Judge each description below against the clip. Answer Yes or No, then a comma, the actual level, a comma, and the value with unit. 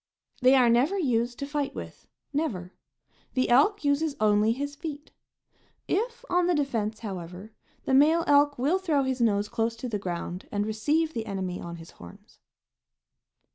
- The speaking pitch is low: No, very high, 255 Hz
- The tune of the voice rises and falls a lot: Yes, wide, 5.8 semitones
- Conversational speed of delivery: Yes, average, 165 wpm